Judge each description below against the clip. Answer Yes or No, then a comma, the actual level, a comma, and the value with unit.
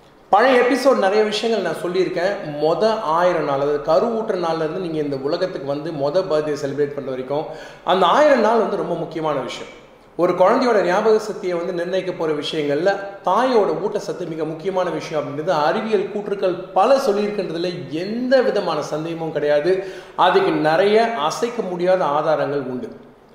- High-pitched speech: No, medium, 180 Hz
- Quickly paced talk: Yes, fast, 145 wpm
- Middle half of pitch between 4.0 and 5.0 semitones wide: Yes, average, 4.7 semitones